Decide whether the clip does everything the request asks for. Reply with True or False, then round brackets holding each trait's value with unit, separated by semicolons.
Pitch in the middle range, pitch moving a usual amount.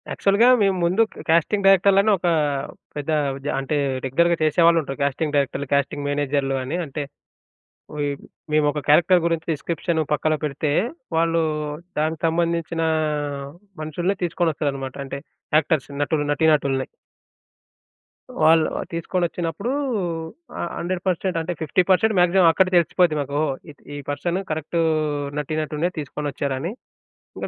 True (160 Hz; 3.2 semitones)